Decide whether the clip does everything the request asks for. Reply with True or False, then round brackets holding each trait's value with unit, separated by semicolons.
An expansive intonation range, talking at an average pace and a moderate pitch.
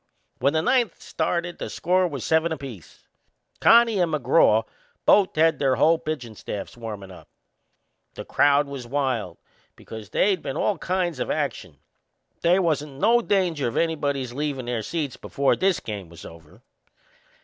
True (6.1 semitones; 155 wpm; 145 Hz)